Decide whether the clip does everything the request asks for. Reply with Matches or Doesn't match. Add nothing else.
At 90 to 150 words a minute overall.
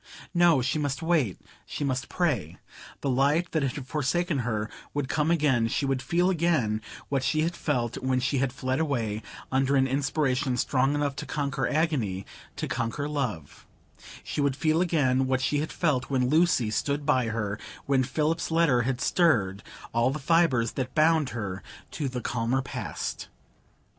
Doesn't match